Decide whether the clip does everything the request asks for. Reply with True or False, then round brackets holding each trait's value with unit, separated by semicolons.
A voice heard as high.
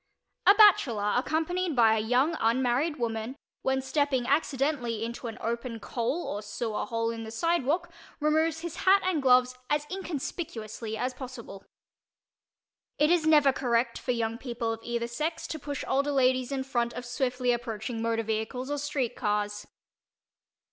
True (250 Hz)